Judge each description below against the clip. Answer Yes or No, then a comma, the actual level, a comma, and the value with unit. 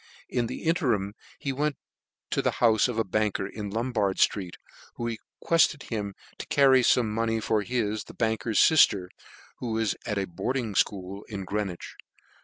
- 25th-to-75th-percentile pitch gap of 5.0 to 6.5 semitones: No, average, 3.6 semitones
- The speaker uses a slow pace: No, average, 165 wpm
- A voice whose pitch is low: Yes, low, 110 Hz